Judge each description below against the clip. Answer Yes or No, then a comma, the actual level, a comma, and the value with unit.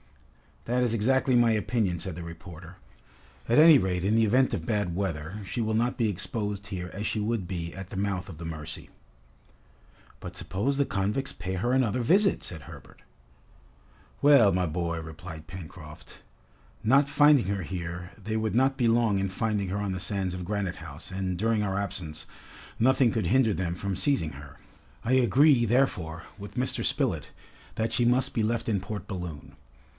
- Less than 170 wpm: No, average, 180 wpm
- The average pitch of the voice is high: No, low, 100 Hz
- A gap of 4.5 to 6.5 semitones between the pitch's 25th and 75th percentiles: Yes, average, 4.9 semitones